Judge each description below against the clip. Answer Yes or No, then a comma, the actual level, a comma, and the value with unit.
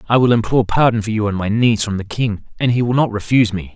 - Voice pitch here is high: No, low, 110 Hz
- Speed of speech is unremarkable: No, fast, 290 wpm